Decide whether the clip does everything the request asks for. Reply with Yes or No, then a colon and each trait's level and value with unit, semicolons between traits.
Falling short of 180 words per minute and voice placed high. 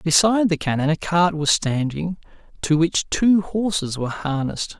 No: average, 165 wpm; medium, 165 Hz